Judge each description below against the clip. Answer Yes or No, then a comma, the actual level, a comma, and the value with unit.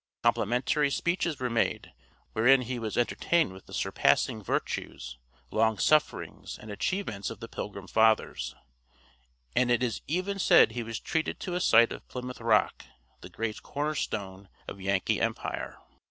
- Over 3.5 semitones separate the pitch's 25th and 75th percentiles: Yes, average, 5.1 semitones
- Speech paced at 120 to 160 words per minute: Yes, average, 155 wpm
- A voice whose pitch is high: No, low, 115 Hz